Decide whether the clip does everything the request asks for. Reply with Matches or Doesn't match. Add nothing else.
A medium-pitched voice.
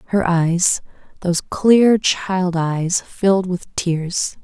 Matches